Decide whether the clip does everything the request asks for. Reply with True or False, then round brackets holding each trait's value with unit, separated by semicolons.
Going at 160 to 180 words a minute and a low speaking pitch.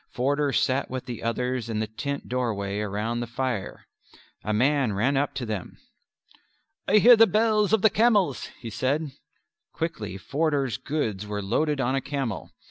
True (165 wpm; 130 Hz)